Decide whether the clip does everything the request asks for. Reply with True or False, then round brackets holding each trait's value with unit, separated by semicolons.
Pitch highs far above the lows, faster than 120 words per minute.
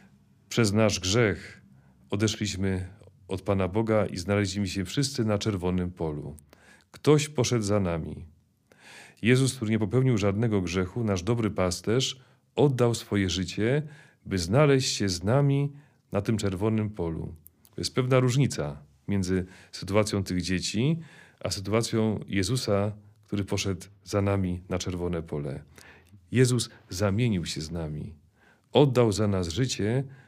False (4.4 semitones; 130 wpm)